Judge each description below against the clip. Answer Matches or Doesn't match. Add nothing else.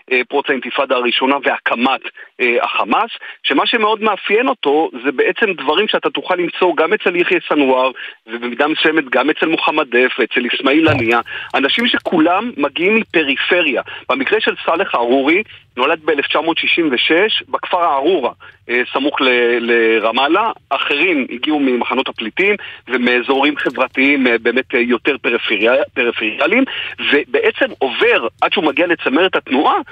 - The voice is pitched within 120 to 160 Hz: Matches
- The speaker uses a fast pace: Doesn't match